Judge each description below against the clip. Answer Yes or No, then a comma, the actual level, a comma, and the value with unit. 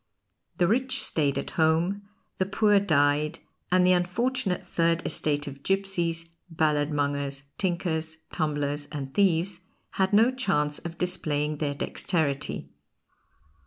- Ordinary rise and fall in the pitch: Yes, average, 4.4 semitones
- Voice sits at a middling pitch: Yes, medium, 165 Hz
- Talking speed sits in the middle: No, slow, 120 wpm